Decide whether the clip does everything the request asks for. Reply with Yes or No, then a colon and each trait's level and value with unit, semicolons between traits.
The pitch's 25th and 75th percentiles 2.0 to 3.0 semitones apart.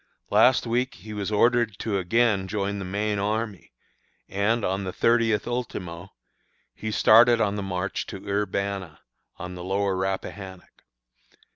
Yes: average, 2.7 semitones